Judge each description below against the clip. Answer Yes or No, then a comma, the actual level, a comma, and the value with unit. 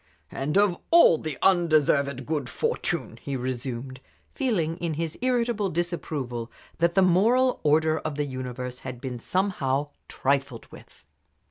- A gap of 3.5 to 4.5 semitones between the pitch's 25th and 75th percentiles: No, average, 5.3 semitones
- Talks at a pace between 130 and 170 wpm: Yes, slow, 135 wpm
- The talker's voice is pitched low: No, medium, 155 Hz